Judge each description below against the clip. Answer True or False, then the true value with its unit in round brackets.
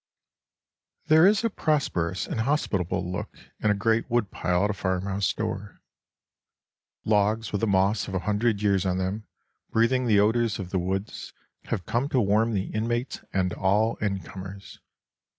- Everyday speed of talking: True (160 wpm)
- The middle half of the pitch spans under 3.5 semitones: True (3.1 semitones)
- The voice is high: False (105 Hz)